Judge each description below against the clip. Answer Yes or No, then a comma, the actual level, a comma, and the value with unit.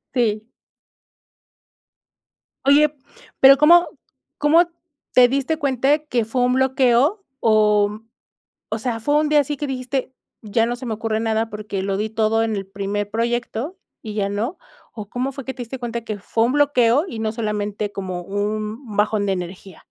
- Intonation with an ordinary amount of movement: Yes, average, 3.9 semitones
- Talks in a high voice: Yes, high, 230 Hz